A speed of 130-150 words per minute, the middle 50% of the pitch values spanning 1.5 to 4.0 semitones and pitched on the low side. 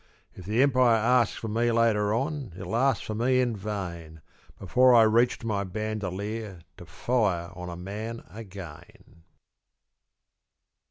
Yes: average, 145 wpm; average, 3.7 semitones; low, 110 Hz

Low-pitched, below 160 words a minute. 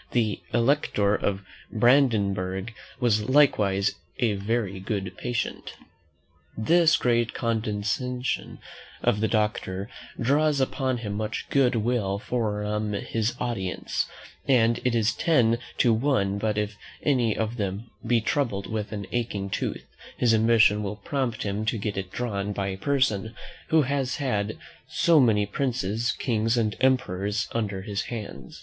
Yes: low, 110 Hz; average, 140 wpm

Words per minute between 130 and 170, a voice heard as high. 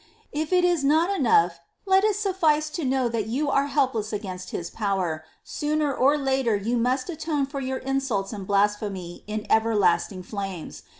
No: average, 180 wpm; very high, 260 Hz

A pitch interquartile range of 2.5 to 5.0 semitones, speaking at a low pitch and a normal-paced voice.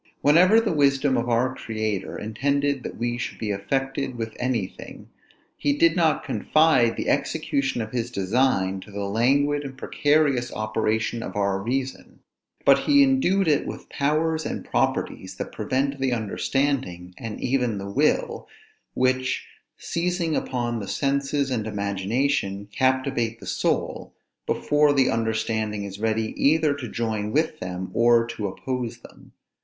Yes: average, 4.6 semitones; low, 125 Hz; average, 145 wpm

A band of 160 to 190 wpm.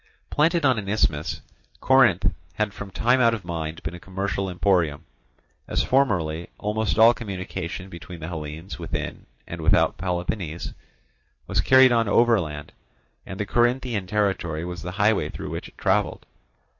No: average, 150 wpm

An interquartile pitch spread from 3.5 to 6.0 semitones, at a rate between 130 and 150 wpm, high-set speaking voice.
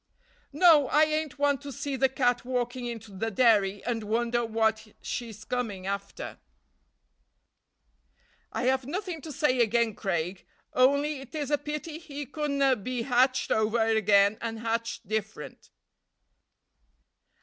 Yes: average, 4.2 semitones; slow, 135 wpm; high, 245 Hz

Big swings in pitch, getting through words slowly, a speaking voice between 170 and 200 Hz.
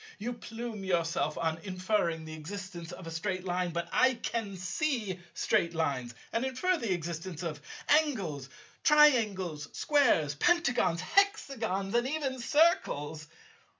Yes: wide, 6.8 semitones; slow, 130 wpm; high, 190 Hz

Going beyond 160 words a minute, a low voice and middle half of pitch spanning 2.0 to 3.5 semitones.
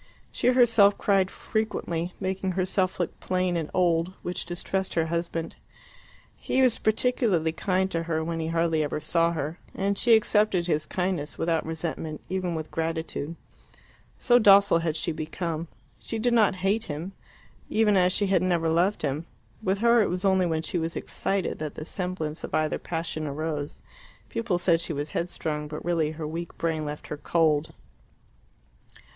No: average, 170 wpm; medium, 170 Hz; average, 3.1 semitones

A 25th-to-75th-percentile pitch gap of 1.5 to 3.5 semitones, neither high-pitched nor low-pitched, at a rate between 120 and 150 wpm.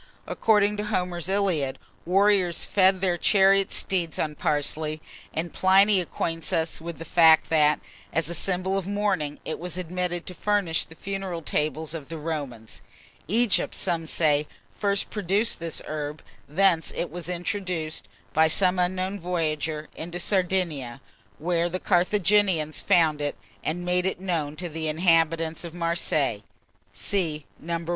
Yes: average, 3.1 semitones; medium, 170 Hz; average, 145 wpm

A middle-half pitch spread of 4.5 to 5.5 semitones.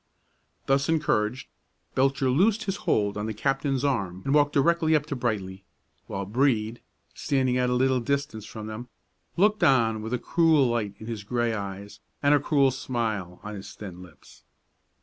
Yes: average, 4.8 semitones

